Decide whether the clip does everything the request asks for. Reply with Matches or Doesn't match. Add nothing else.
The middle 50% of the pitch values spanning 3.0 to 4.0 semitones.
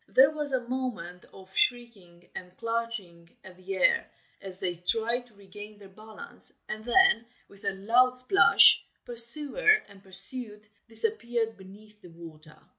Doesn't match